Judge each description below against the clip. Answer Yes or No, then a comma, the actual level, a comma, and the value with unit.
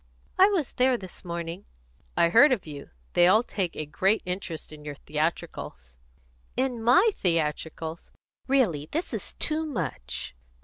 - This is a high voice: No, medium, 175 Hz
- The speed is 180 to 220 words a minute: No, average, 150 wpm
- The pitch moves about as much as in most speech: No, wide, 8.3 semitones